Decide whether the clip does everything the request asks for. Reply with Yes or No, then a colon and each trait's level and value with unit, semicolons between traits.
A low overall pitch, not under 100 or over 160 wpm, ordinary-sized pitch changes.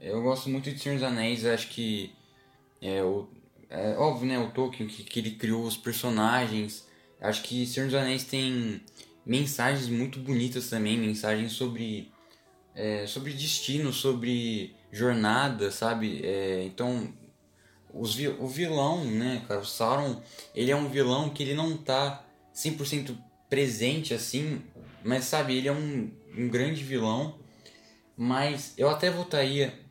Yes: low, 125 Hz; average, 145 wpm; average, 3.7 semitones